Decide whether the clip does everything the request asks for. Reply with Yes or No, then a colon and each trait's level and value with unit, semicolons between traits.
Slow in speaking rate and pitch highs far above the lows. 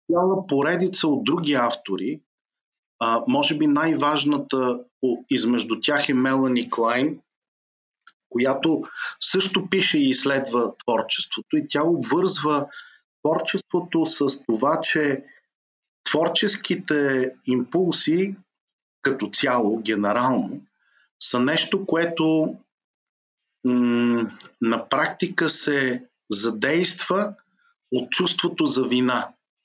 Yes: slow, 90 wpm; wide, 6.3 semitones